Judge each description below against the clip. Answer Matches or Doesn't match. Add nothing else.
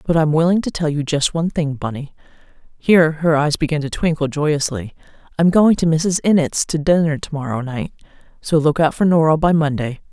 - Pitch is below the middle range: Doesn't match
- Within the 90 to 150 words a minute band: Doesn't match